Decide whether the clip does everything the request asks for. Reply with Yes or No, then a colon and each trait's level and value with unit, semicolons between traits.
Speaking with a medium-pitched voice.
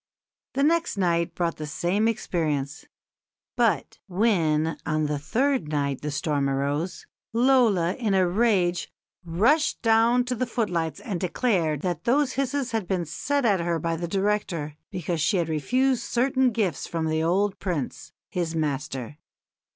Yes: medium, 180 Hz